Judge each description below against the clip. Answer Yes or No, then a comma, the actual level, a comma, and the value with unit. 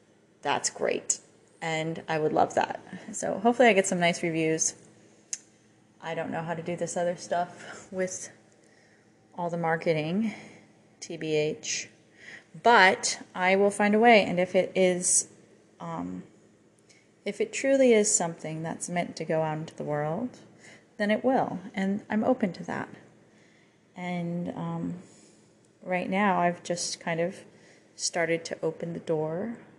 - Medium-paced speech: Yes, average, 145 wpm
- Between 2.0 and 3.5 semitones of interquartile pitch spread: No, average, 3.9 semitones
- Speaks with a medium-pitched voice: Yes, medium, 175 Hz